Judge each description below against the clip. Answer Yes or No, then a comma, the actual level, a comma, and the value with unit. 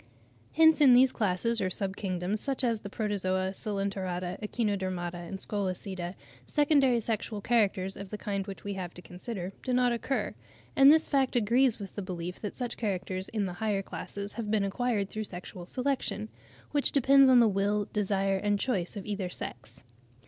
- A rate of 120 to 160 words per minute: No, average, 175 wpm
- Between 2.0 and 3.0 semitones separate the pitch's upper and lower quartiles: No, average, 4.0 semitones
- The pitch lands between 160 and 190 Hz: No, high, 205 Hz